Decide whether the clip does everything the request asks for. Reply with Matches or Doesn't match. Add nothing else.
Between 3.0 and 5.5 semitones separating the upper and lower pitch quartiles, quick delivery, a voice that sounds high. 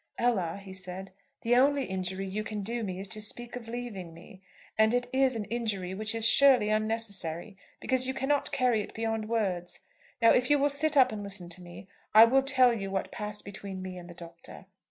Matches